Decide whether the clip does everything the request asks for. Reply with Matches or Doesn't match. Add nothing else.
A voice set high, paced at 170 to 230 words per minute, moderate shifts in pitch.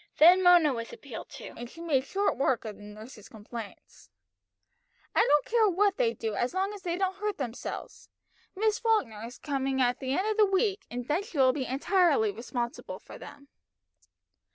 Doesn't match